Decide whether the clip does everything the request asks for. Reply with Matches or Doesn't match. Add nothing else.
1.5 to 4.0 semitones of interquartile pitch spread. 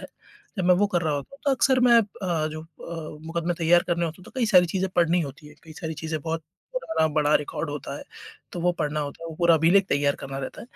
Matches